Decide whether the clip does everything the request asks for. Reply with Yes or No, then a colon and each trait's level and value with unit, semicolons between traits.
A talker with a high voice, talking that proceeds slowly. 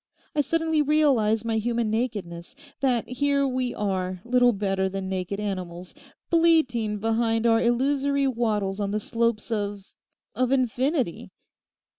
Yes: high, 230 Hz; slow, 125 wpm